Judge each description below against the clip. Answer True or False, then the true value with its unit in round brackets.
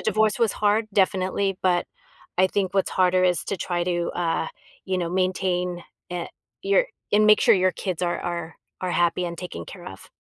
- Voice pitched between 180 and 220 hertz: True (185 Hz)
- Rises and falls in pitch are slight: True (1.9 semitones)